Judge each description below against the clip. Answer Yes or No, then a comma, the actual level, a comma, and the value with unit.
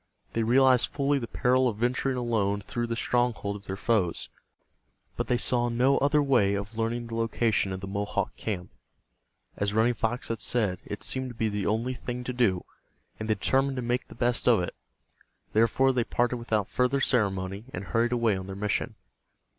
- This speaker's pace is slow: No, average, 195 wpm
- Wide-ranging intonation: No, average, 3.3 semitones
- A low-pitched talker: Yes, low, 115 Hz